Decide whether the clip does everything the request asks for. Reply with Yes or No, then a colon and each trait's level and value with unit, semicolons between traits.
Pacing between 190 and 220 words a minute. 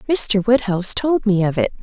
Yes: average, 200 wpm